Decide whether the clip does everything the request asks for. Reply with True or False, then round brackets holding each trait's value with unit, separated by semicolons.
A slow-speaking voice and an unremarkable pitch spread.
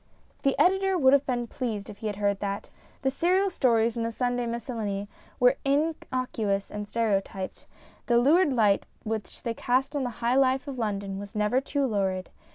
False (180 wpm; 4.4 semitones)